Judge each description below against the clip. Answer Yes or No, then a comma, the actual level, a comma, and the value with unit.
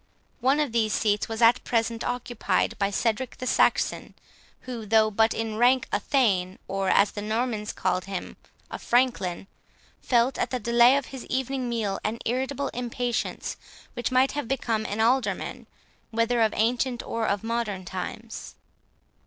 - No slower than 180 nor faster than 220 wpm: No, average, 160 wpm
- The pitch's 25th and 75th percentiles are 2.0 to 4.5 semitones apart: Yes, average, 2.7 semitones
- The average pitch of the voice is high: Yes, high, 230 Hz